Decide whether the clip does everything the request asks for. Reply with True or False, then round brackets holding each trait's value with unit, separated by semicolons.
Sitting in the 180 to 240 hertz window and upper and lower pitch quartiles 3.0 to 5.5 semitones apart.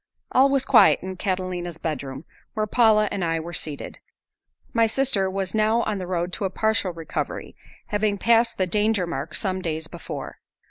True (190 Hz; 4.0 semitones)